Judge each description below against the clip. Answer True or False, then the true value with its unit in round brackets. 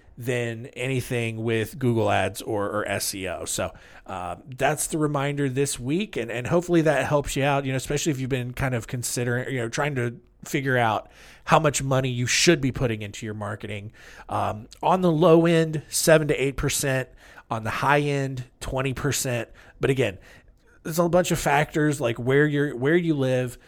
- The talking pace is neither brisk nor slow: True (190 wpm)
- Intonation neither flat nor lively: True (3.5 semitones)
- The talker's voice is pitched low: True (130 Hz)